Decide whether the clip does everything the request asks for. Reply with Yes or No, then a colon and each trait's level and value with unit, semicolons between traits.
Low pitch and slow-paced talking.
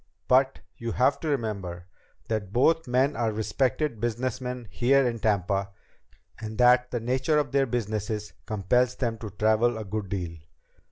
No: low, 115 Hz; average, 155 wpm